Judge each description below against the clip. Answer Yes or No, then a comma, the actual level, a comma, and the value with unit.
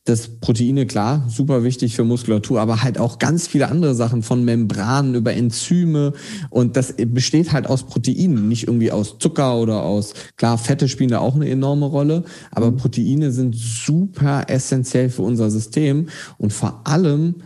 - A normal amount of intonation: Yes, average, 3.6 semitones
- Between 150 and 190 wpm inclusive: Yes, average, 170 wpm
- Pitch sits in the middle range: No, low, 130 Hz